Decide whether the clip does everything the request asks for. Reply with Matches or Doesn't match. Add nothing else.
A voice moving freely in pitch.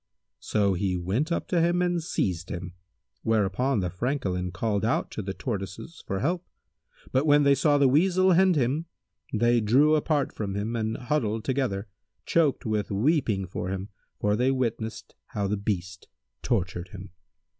Matches